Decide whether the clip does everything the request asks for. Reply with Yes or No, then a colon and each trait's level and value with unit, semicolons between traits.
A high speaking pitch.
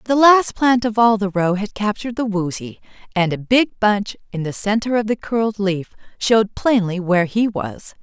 Yes: high, 210 Hz